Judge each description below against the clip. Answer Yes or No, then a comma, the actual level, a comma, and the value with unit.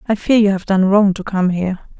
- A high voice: Yes, high, 195 Hz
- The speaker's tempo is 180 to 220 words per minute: No, fast, 270 wpm